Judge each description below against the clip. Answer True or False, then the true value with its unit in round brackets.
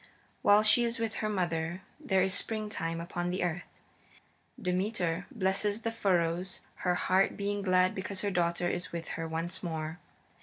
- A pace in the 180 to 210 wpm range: False (160 wpm)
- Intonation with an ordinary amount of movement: True (3.0 semitones)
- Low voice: False (185 Hz)